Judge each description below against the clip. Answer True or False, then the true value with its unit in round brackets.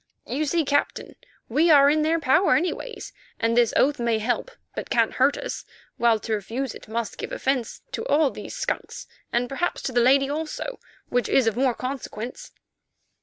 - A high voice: True (270 Hz)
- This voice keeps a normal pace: True (180 wpm)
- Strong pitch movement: False (4.5 semitones)